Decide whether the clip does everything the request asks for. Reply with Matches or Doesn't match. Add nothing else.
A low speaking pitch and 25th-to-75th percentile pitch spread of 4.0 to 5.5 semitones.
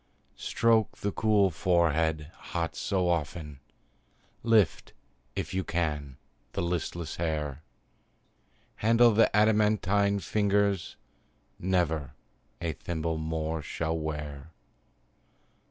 Matches